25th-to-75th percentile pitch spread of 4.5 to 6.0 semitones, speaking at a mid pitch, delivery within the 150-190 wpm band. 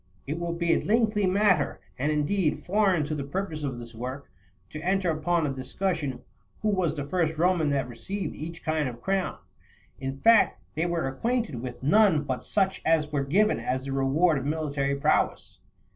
Yes: average, 5.2 semitones; medium, 155 Hz; average, 185 wpm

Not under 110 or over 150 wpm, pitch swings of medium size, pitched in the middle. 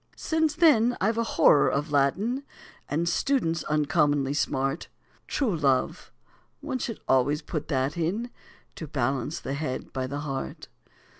No: average, 140 wpm; wide, 8.4 semitones; medium, 150 Hz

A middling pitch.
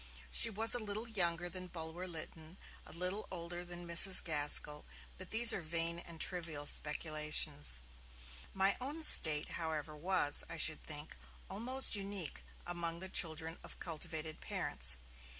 Yes: medium, 170 Hz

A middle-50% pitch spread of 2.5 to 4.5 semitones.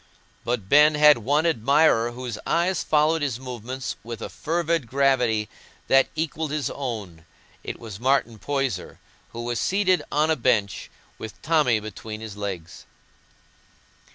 No: average, 5.2 semitones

